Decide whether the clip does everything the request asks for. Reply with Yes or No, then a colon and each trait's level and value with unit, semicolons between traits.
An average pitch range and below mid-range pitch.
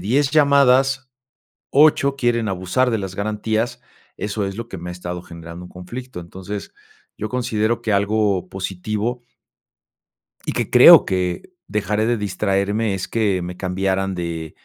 Yes: average, 4.2 semitones; low, 105 Hz